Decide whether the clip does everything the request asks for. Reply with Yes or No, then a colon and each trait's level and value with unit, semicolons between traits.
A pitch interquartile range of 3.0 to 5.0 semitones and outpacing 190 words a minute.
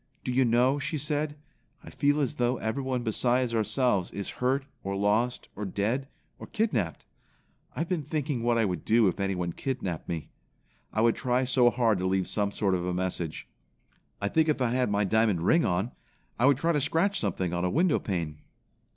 No: wide, 5.5 semitones; average, 200 wpm